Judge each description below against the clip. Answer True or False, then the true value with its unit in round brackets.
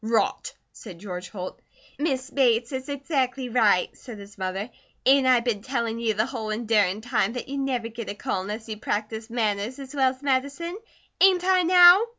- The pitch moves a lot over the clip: False (4.1 semitones)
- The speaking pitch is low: False (235 Hz)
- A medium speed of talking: True (185 wpm)